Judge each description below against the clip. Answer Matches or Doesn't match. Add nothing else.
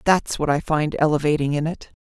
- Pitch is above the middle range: Doesn't match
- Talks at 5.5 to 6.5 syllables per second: Matches